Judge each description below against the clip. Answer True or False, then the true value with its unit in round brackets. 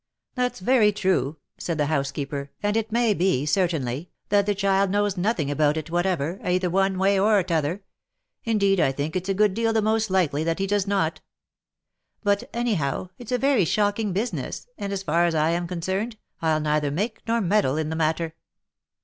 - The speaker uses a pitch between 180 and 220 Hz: True (190 Hz)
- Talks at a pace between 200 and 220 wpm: True (205 wpm)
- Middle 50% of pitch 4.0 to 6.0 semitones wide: True (4.5 semitones)